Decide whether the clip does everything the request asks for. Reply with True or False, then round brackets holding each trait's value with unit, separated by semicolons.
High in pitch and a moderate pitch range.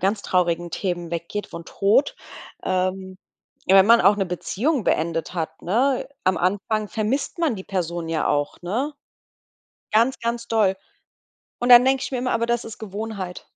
True (200 Hz; 4.7 semitones)